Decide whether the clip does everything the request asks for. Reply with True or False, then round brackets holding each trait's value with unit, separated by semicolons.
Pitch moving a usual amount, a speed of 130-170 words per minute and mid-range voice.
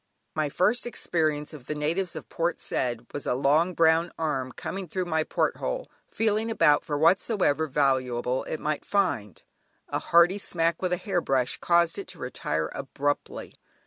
True (4.2 semitones; 165 wpm; 160 Hz)